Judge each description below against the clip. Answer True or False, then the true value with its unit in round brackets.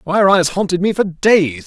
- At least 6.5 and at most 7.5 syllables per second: False (5.1 syllables/s)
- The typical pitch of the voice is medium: True (180 Hz)